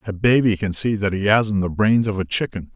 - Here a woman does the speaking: No, male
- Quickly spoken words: Yes, fast, 260 wpm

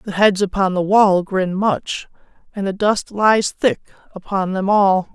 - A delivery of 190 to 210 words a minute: No, average, 175 wpm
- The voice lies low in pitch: No, high, 195 Hz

